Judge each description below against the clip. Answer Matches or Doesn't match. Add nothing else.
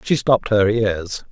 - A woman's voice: Doesn't match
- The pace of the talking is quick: Doesn't match